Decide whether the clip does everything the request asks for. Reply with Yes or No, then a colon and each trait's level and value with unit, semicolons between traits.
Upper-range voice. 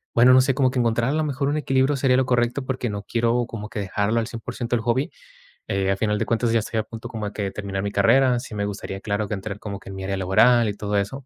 No: low, 115 Hz